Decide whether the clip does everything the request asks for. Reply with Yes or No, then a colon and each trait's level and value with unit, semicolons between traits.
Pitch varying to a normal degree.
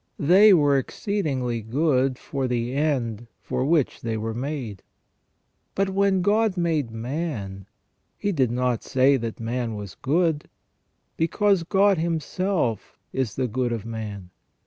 No: wide, 6.4 semitones